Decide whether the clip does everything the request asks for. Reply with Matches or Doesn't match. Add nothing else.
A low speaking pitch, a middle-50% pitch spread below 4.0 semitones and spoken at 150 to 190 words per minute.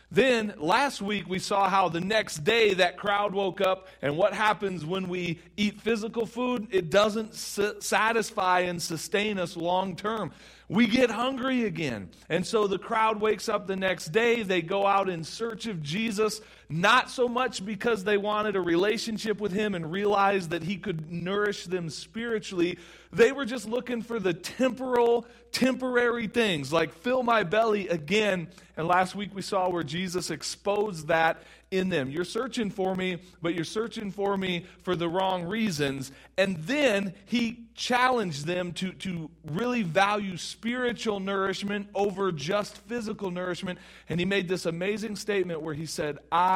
Doesn't match